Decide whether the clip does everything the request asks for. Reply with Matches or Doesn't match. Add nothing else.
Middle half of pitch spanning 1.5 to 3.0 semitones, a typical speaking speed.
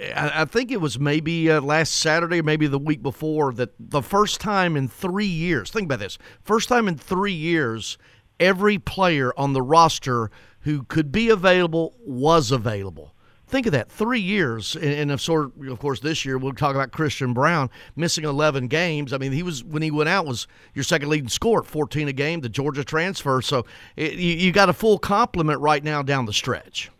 Doesn't match